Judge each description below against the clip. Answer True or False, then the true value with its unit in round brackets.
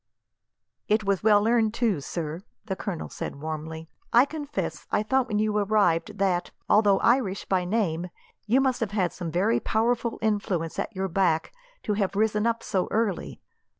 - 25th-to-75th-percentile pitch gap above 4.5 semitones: False (3.7 semitones)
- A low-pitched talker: False (205 Hz)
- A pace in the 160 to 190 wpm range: True (165 wpm)